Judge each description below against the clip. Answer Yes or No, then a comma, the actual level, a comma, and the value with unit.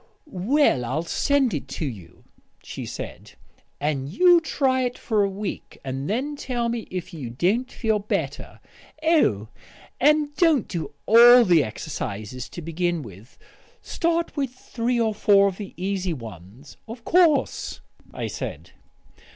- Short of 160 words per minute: Yes, average, 145 wpm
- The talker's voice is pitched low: No, high, 200 Hz